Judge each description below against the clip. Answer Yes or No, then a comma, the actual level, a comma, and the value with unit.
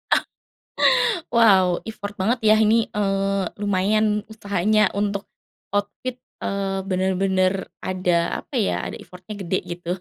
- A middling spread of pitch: No, narrow, 2.2 semitones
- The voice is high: Yes, high, 195 Hz